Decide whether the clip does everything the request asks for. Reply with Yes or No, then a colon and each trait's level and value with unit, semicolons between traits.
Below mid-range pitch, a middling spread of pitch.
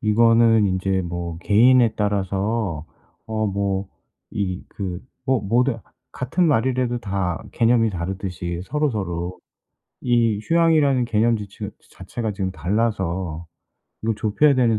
Yes: low, 105 Hz; average, 3.9 semitones